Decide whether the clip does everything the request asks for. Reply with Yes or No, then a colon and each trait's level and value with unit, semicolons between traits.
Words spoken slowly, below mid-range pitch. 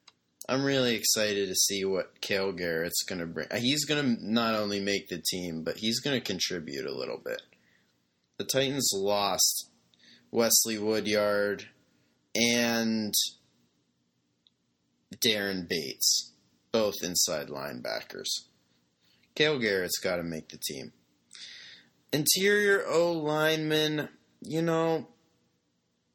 Yes: slow, 105 wpm; low, 100 Hz